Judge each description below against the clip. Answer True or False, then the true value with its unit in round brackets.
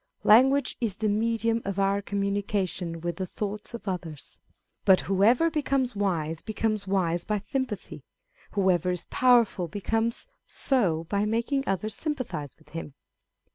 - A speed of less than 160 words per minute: True (135 wpm)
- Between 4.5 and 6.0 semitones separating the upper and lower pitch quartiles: False (4.1 semitones)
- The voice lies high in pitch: True (200 Hz)